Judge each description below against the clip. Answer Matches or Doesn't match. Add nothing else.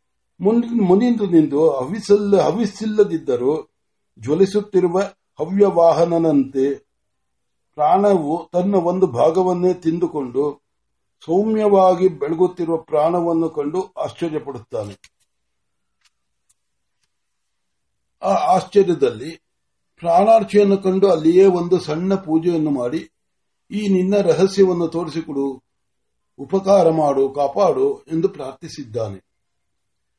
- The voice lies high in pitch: Doesn't match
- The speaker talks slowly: Matches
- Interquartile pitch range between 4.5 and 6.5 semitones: Matches